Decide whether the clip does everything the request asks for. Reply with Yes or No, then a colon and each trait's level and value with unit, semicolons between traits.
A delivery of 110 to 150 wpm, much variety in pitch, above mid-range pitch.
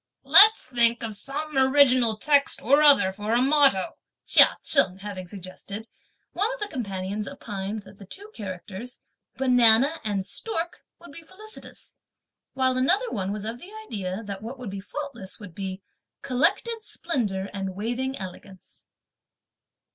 Yes: average, 145 wpm; wide, 6.2 semitones; high, 235 Hz